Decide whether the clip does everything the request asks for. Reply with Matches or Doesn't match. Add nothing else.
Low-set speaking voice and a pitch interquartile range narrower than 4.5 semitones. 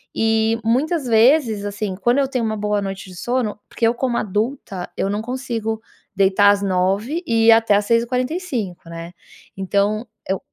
Doesn't match